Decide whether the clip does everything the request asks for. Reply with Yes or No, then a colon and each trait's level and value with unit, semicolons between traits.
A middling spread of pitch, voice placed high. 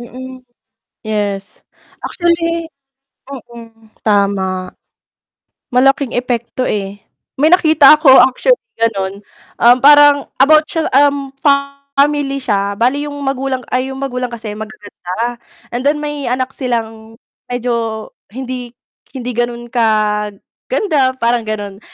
Yes: average, 4.1 semitones; high, 245 Hz